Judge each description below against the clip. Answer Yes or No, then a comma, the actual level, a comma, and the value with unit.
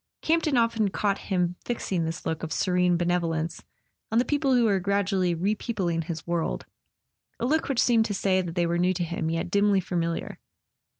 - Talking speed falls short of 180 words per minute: No, average, 185 wpm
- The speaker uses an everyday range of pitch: Yes, average, 4.0 semitones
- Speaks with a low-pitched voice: No, medium, 185 Hz